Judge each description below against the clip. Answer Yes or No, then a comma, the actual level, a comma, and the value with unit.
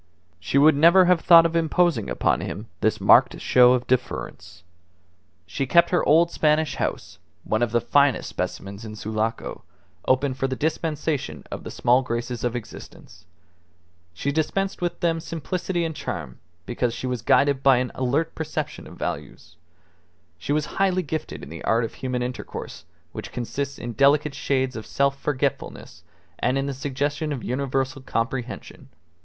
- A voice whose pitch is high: No, low, 135 Hz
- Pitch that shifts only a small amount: No, average, 4.2 semitones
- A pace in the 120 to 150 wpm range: No, average, 160 wpm